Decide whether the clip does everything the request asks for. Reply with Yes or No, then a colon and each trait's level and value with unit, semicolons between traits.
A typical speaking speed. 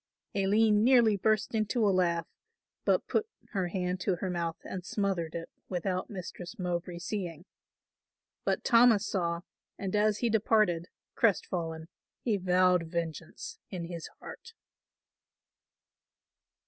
No: slow, 125 wpm